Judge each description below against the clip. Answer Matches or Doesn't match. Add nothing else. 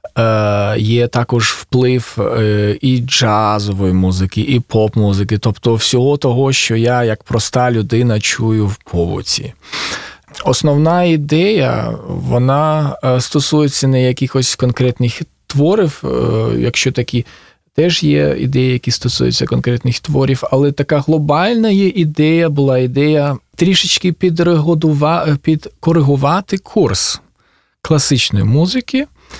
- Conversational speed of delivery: Doesn't match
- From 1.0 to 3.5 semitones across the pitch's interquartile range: Doesn't match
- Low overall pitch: Matches